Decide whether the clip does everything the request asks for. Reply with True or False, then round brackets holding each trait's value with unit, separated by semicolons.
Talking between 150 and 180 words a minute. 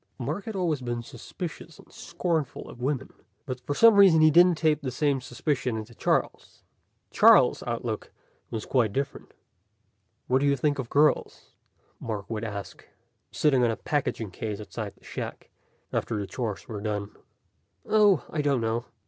True (165 wpm)